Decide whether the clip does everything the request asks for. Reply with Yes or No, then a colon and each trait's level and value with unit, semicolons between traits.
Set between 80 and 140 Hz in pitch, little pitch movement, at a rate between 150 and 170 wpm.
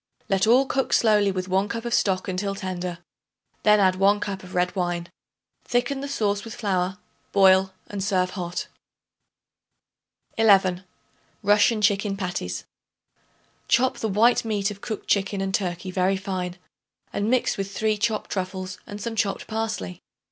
No: high, 195 Hz; narrow, 2.3 semitones; average, 155 wpm